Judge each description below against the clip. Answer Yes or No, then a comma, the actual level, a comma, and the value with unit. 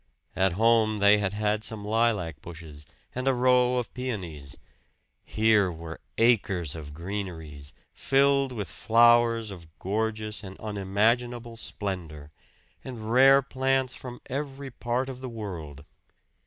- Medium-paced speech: No, slow, 130 wpm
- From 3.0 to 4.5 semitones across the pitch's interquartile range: No, average, 5.0 semitones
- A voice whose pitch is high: No, low, 110 Hz